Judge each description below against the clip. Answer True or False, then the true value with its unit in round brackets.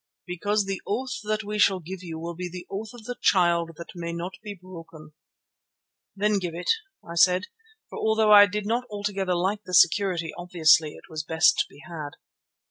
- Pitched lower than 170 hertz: False (185 Hz)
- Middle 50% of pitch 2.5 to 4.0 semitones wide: True (3.5 semitones)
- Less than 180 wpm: False (200 wpm)